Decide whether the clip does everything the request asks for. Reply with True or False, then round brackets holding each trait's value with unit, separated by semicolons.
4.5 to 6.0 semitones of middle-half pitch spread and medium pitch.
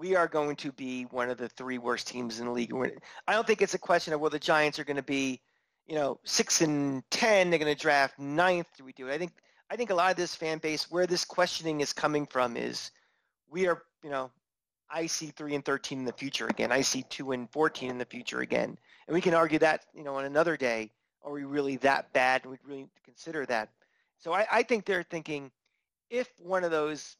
False (4.1 semitones; 145 Hz)